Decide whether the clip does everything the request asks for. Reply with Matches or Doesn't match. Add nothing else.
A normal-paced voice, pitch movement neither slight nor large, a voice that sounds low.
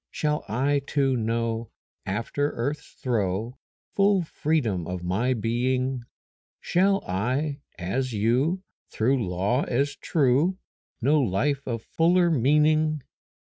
Doesn't match